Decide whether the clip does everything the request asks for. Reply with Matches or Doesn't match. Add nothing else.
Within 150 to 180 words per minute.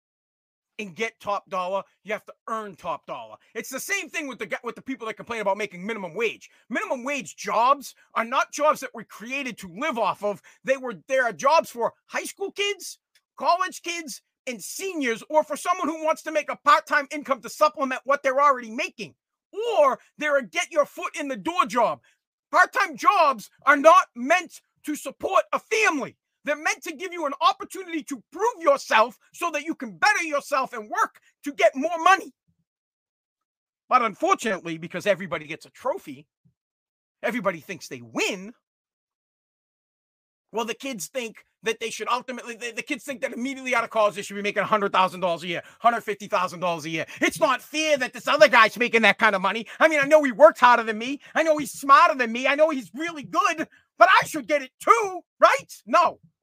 Doesn't match